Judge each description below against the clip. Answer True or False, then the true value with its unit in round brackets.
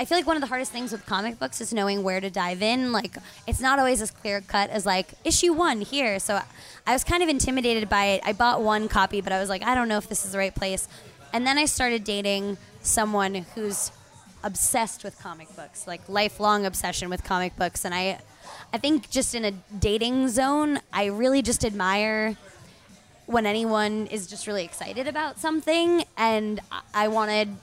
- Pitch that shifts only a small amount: False (4.0 semitones)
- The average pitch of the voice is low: False (215 Hz)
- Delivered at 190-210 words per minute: True (205 wpm)